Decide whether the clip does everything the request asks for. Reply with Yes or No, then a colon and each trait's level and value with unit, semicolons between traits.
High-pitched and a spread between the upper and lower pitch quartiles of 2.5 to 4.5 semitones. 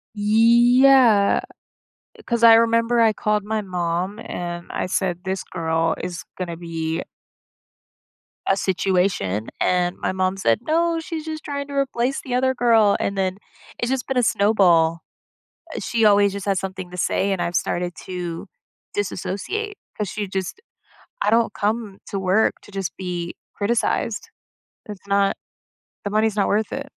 Yes: high, 200 Hz; average, 4.2 semitones